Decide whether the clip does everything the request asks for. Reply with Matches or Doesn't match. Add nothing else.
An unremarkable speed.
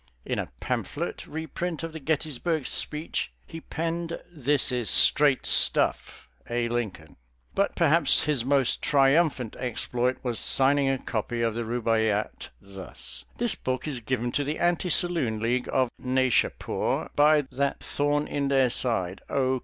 Matches